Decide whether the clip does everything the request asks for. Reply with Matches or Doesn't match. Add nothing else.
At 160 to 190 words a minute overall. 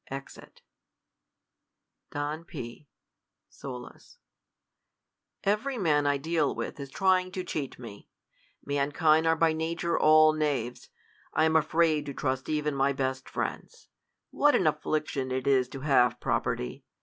Doesn't match